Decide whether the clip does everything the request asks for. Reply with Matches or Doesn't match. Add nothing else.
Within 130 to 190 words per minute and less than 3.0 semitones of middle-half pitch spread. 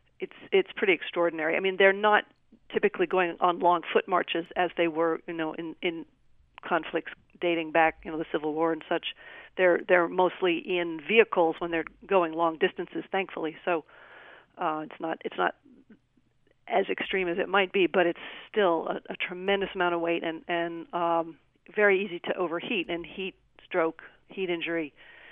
Matches